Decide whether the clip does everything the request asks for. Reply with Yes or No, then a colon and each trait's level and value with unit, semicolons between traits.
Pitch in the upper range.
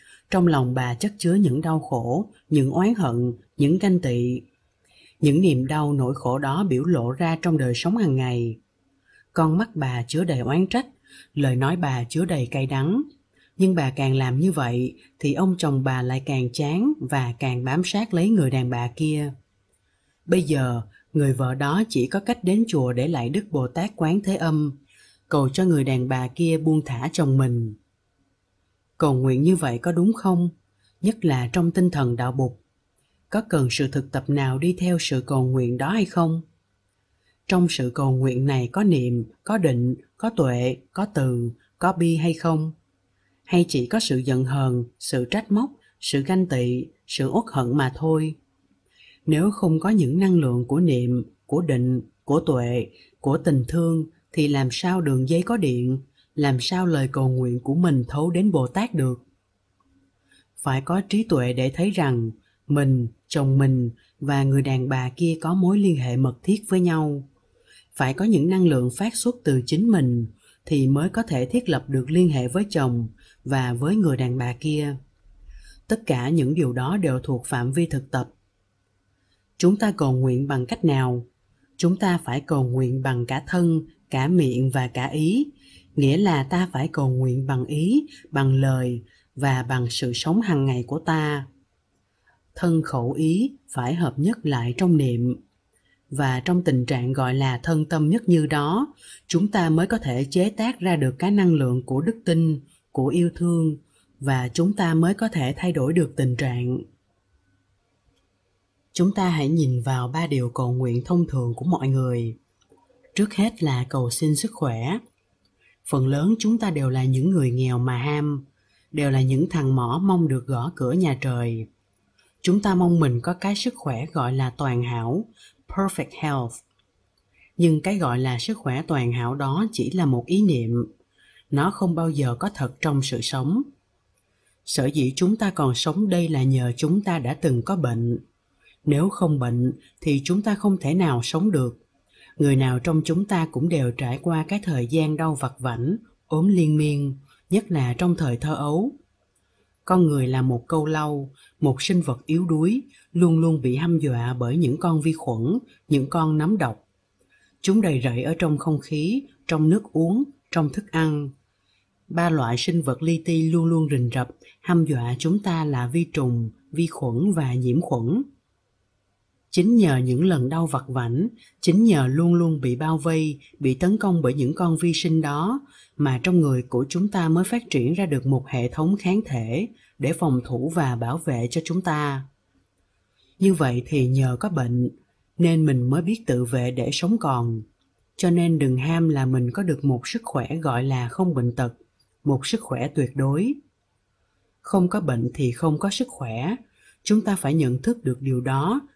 No: medium, 140 Hz